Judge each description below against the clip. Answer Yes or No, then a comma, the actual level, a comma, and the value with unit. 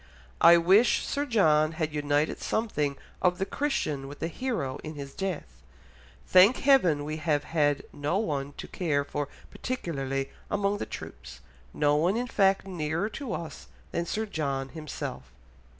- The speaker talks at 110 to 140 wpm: No, average, 155 wpm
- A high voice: No, medium, 160 Hz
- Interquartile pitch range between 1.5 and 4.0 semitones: No, average, 5.1 semitones